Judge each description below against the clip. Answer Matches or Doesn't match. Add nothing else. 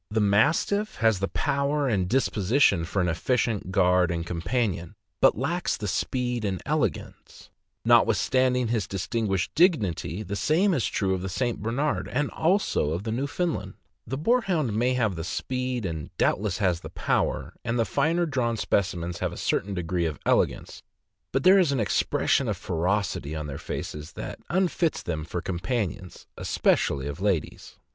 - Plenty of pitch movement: Matches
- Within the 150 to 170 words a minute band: Matches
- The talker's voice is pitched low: Matches